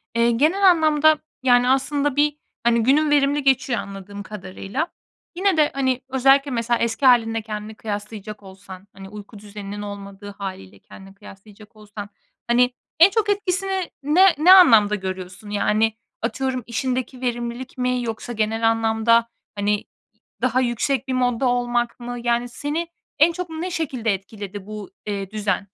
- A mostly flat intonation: No, average, 4.6 semitones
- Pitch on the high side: Yes, high, 235 Hz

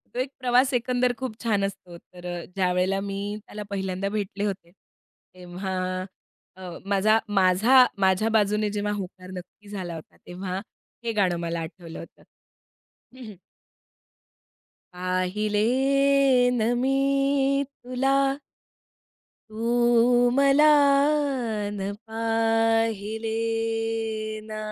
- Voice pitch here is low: No, high, 210 Hz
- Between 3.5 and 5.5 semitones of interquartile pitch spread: Yes, average, 3.9 semitones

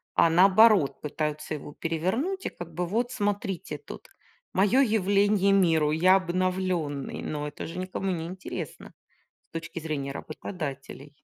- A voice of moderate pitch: Yes, medium, 180 Hz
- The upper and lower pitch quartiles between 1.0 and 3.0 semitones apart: No, average, 4.3 semitones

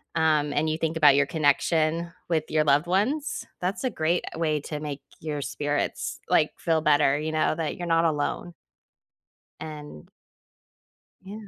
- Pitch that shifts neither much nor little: No, narrow, 2.1 semitones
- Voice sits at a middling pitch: Yes, medium, 155 Hz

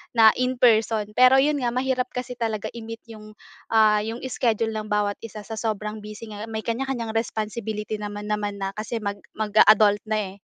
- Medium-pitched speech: No, high, 220 Hz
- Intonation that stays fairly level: Yes, narrow, 1.7 semitones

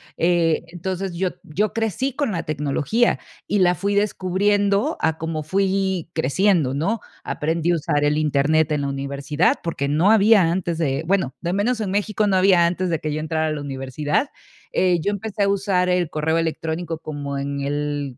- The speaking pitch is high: No, medium, 170 Hz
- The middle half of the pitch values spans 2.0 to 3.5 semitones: No, average, 4.6 semitones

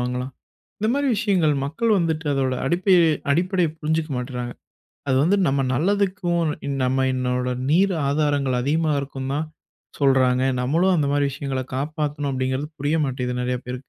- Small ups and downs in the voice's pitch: No, average, 4.0 semitones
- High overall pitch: No, medium, 145 Hz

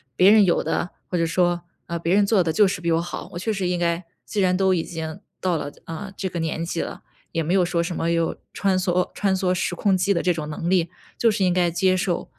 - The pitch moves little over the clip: Yes, narrow, 2.0 semitones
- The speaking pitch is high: No, medium, 180 Hz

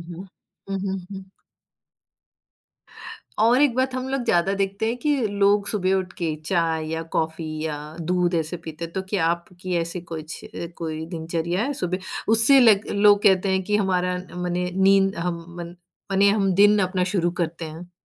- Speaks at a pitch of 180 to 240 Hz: Yes, medium, 185 Hz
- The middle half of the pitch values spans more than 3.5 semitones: No, average, 3.0 semitones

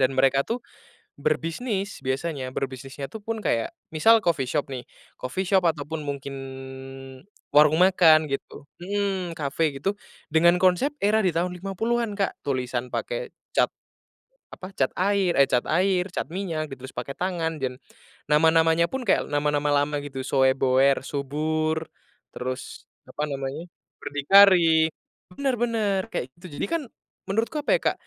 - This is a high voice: No, medium, 160 Hz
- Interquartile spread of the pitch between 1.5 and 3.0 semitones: No, wide, 5.6 semitones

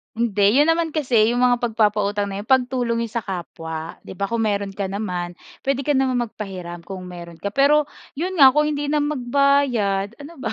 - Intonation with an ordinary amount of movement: No, wide, 5.8 semitones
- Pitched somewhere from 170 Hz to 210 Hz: No, high, 230 Hz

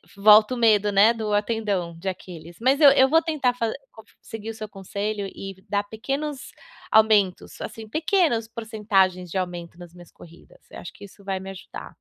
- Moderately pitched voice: No, high, 210 Hz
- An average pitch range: Yes, average, 3.1 semitones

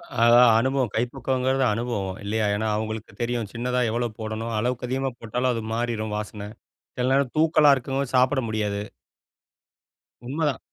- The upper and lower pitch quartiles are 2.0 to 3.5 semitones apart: Yes, average, 3.1 semitones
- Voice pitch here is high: No, low, 120 Hz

